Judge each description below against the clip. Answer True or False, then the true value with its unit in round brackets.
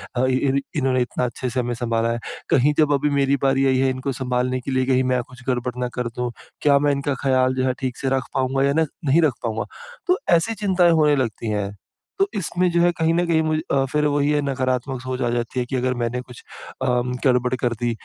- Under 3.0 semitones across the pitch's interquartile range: True (2.4 semitones)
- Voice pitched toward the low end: True (130 Hz)